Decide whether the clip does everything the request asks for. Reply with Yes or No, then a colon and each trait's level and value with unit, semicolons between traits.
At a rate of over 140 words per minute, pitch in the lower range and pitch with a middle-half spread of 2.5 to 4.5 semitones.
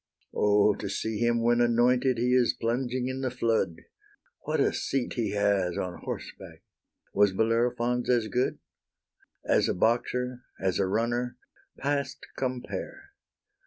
No: slow, 135 wpm; low, 120 Hz; average, 2.9 semitones